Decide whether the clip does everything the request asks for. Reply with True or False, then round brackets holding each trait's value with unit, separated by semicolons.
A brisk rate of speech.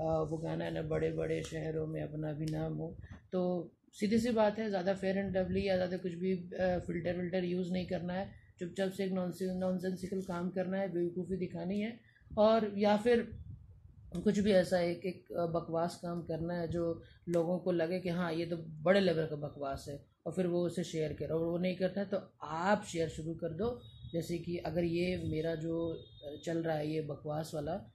True (210 wpm)